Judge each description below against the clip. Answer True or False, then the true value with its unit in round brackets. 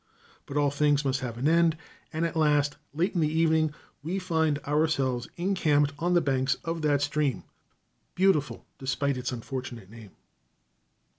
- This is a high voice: False (150 Hz)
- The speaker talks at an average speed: True (155 wpm)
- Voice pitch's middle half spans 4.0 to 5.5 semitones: False (3.3 semitones)